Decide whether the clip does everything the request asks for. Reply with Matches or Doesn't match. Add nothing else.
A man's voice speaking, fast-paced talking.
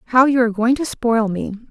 Doesn't match